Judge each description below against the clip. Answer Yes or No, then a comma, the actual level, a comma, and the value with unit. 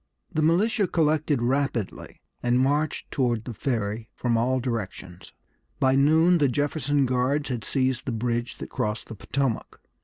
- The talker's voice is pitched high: No, low, 130 Hz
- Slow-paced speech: No, average, 150 wpm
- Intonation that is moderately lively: Yes, average, 3.7 semitones